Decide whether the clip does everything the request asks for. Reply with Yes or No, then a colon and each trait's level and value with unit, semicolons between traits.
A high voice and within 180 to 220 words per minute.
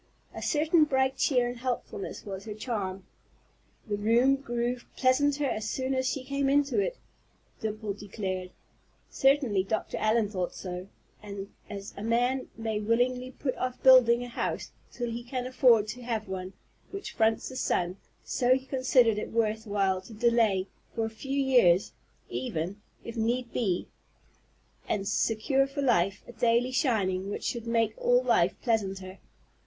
No: high, 230 Hz; average, 160 wpm